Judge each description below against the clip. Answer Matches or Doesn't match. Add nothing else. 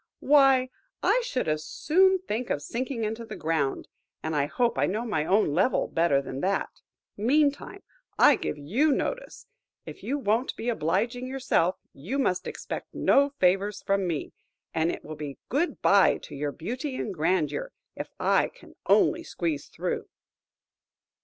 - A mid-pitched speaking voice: Doesn't match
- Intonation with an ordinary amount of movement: Doesn't match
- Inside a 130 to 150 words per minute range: Doesn't match